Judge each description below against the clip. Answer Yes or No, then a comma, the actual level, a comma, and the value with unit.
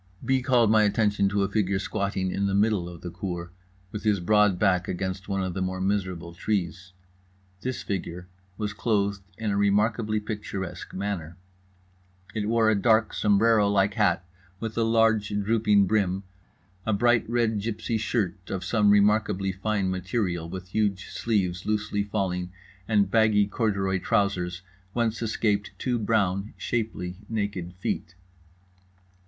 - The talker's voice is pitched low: Yes, low, 100 Hz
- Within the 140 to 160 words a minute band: Yes, average, 150 wpm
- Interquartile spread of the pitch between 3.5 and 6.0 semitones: No, narrow, 2.6 semitones